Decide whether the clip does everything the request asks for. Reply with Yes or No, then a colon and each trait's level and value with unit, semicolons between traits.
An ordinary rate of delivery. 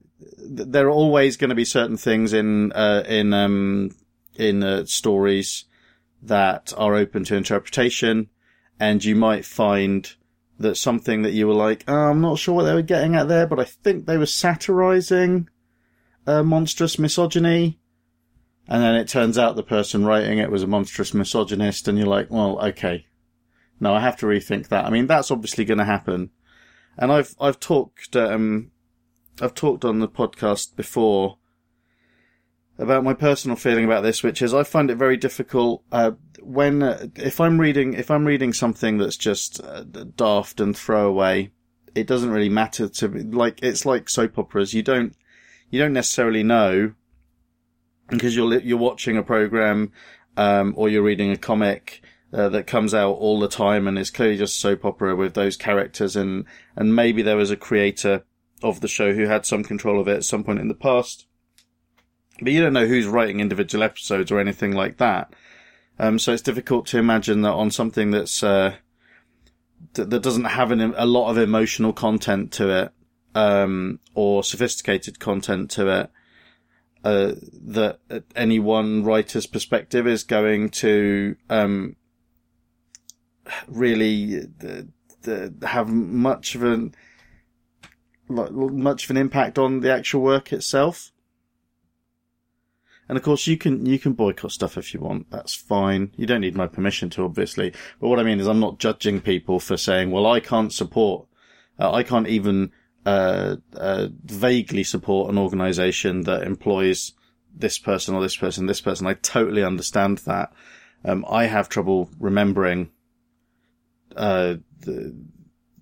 Yes: average, 165 wpm